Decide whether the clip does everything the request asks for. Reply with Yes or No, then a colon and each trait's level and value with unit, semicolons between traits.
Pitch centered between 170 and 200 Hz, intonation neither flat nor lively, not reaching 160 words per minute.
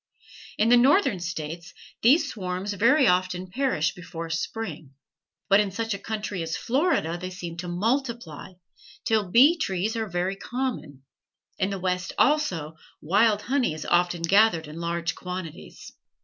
Yes: medium, 185 Hz; average, 4.9 semitones; average, 150 wpm